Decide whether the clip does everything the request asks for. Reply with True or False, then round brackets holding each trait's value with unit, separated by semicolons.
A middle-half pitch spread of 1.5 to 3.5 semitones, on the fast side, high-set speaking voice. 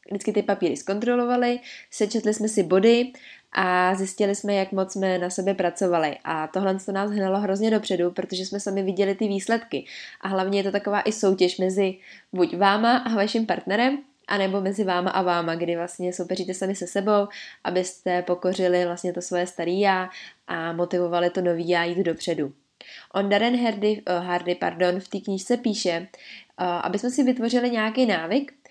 True (2.6 semitones; 180 wpm; 195 Hz)